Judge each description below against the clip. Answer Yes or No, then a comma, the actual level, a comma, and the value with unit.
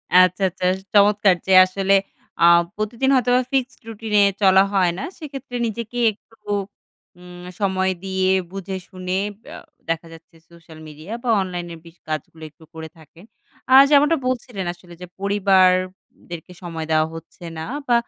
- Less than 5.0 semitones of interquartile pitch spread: Yes, average, 3.6 semitones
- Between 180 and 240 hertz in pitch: Yes, high, 190 Hz